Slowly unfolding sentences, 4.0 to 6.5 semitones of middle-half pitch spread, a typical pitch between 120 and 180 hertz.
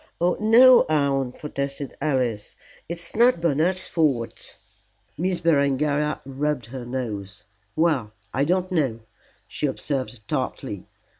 Yes: slow, 120 wpm; average, 4.6 semitones; medium, 140 Hz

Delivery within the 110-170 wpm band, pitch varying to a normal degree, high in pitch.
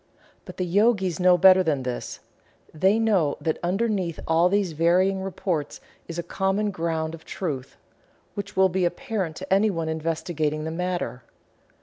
No: average, 155 wpm; average, 3.1 semitones; medium, 180 Hz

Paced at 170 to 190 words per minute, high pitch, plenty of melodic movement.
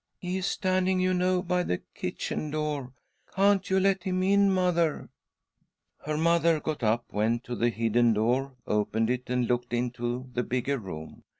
No: average, 175 wpm; medium, 140 Hz; wide, 7.3 semitones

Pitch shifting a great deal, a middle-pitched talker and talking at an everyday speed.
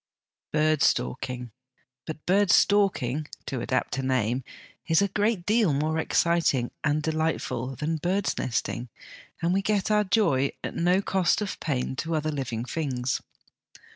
Yes: wide, 6.1 semitones; medium, 155 Hz; average, 145 wpm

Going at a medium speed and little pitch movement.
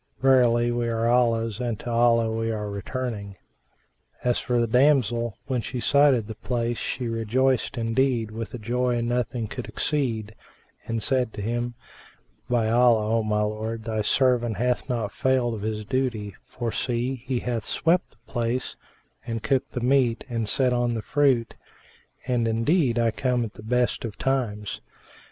Yes: average, 165 wpm; narrow, 1.9 semitones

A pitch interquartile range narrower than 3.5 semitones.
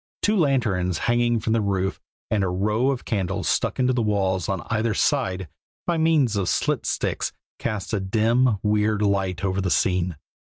No: average, 3.8 semitones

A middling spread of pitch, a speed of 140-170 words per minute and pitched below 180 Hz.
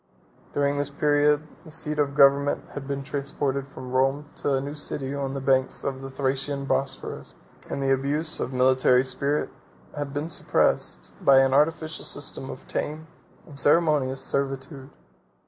No: narrow, 1.5 semitones; average, 160 wpm; medium, 140 Hz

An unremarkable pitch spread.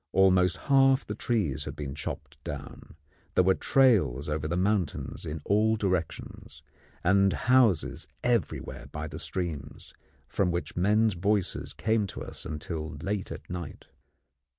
Yes: average, 5.0 semitones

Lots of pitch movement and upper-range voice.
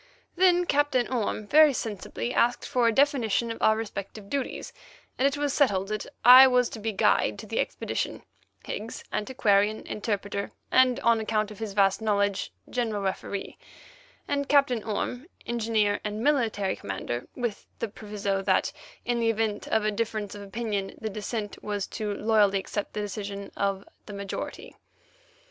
No: average, 3.0 semitones; high, 215 Hz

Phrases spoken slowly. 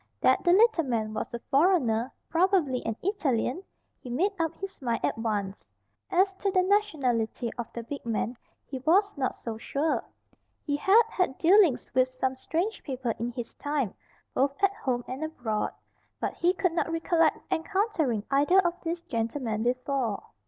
No: average, 165 wpm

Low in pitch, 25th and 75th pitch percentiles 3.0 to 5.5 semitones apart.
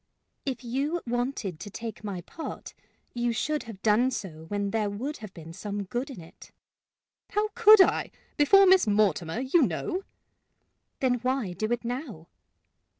No: high, 235 Hz; average, 5.2 semitones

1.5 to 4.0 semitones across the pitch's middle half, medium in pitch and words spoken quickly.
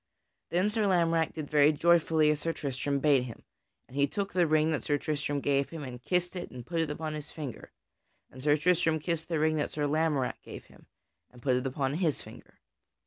Yes: average, 2.7 semitones; medium, 155 Hz; fast, 215 wpm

